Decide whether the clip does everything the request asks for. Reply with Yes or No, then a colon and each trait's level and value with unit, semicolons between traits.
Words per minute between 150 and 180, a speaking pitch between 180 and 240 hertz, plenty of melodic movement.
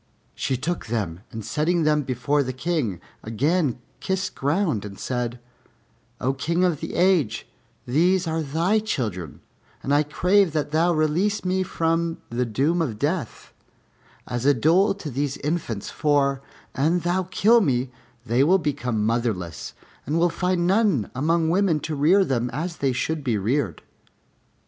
No: average, 155 wpm; medium, 150 Hz; wide, 5.7 semitones